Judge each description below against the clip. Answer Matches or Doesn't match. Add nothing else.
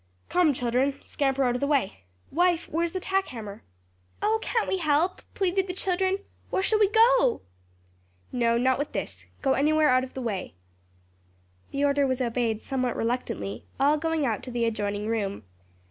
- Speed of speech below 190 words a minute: Matches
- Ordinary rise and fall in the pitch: Doesn't match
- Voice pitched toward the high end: Matches